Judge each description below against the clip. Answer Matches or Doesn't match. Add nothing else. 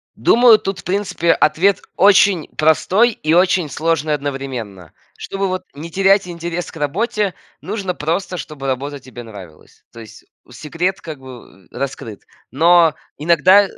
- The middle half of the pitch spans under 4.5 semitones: Doesn't match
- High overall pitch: Doesn't match